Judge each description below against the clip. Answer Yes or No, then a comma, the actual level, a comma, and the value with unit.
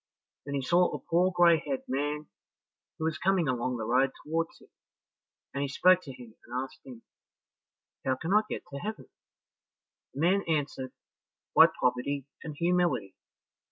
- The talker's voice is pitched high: No, medium, 145 Hz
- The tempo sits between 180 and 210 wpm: No, average, 160 wpm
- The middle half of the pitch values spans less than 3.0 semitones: No, average, 4.7 semitones